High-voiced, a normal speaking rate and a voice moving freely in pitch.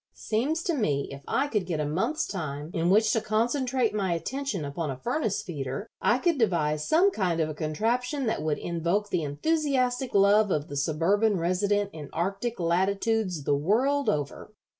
Yes: high, 200 Hz; average, 180 wpm; wide, 7.3 semitones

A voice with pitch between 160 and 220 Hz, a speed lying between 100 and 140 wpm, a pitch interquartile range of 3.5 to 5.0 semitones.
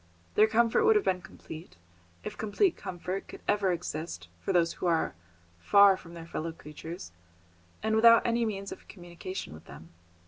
No: medium, 185 Hz; average, 170 wpm; average, 4.6 semitones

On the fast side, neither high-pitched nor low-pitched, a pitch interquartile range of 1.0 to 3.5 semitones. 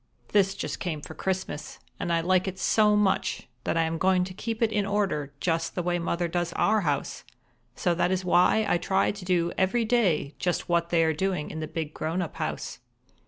Yes: fast, 215 wpm; medium, 180 Hz; average, 2.7 semitones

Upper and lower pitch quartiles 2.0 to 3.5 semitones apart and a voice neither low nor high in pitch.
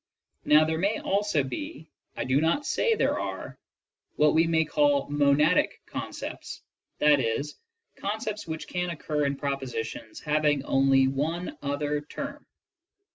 No: average, 4.3 semitones; medium, 150 Hz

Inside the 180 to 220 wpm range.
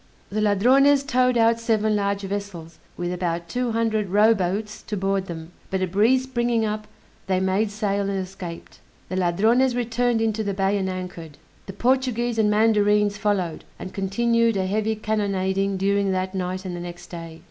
No: average, 170 wpm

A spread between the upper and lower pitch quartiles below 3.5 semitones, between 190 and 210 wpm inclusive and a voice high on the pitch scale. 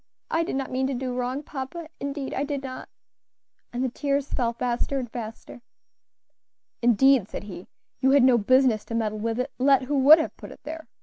Yes: narrow, 2.5 semitones; average, 200 wpm; very high, 260 Hz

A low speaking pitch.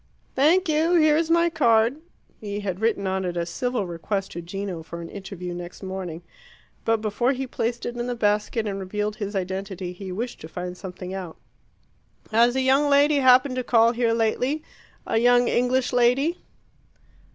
No: high, 225 Hz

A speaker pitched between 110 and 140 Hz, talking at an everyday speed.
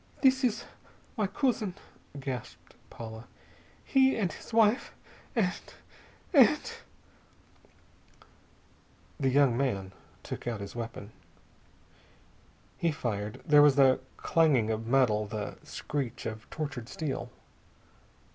No: low, 135 Hz; slow, 110 wpm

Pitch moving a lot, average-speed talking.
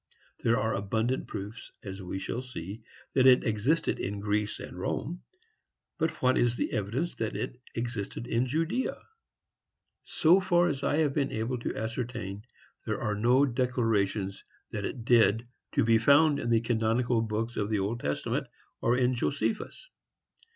No: average, 3.3 semitones; average, 160 wpm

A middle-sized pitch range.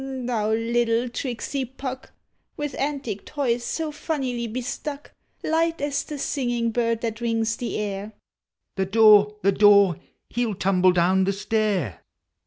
Yes: average, 4.2 semitones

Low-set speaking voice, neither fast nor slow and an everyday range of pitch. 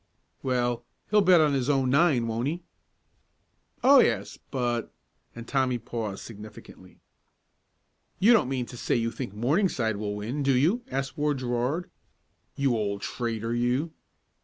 Yes: low, 125 Hz; average, 150 wpm; average, 3.9 semitones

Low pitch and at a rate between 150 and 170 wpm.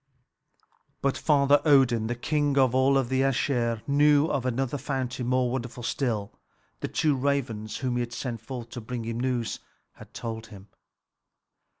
Yes: low, 125 Hz; average, 155 wpm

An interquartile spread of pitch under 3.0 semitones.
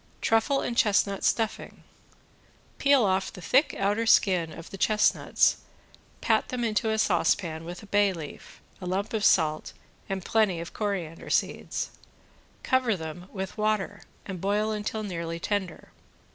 No: average, 3.5 semitones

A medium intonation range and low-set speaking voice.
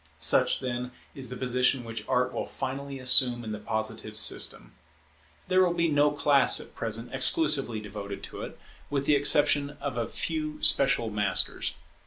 Yes: average, 4.0 semitones; low, 130 Hz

